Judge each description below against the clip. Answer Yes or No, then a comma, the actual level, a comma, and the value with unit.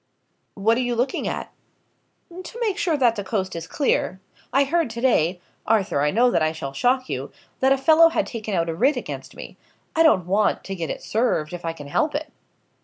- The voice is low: No, high, 230 Hz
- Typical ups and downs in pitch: No, wide, 7.5 semitones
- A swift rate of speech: Yes, fast, 220 wpm